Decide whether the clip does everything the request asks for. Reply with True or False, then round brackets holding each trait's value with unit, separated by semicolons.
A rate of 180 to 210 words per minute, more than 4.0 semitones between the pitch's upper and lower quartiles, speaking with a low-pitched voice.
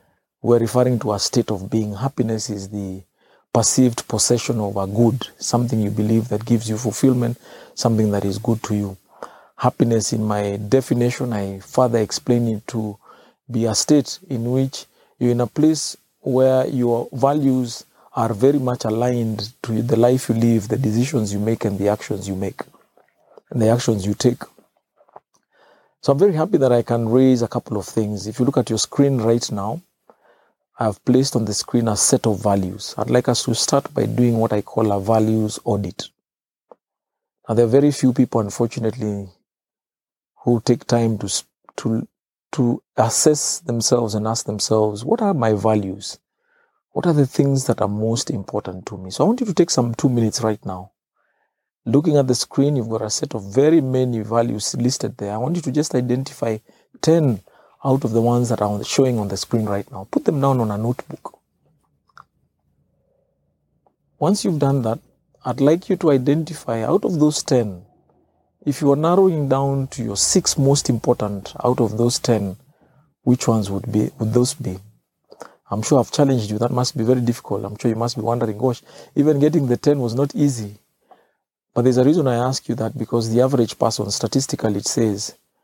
False (190 wpm; 3.6 semitones; 120 Hz)